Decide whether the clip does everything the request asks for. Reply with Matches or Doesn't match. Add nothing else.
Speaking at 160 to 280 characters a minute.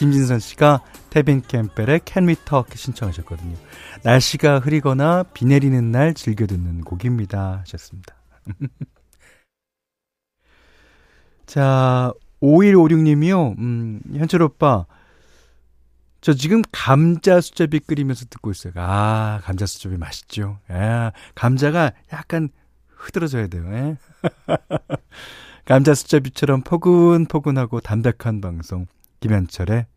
Matches